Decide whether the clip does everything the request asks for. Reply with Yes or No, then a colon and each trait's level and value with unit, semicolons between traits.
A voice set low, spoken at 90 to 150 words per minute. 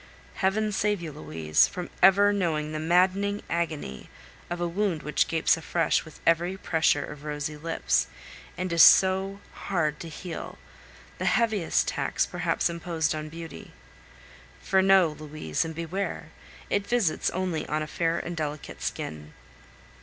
No: medium, 165 Hz; average, 145 wpm